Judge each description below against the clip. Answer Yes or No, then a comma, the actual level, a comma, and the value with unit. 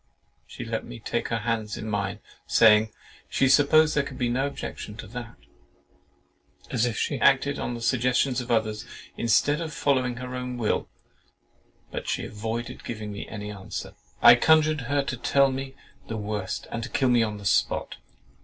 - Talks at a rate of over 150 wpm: Yes, average, 170 wpm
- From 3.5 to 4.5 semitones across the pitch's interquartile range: Yes, average, 3.8 semitones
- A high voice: No, low, 120 Hz